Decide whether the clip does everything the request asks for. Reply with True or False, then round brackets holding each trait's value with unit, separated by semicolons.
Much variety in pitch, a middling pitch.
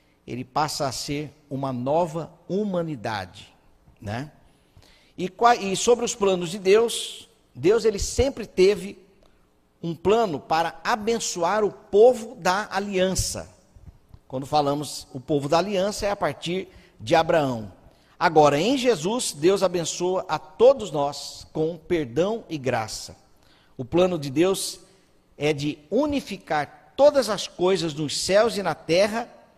True (6.0 semitones; 175 Hz)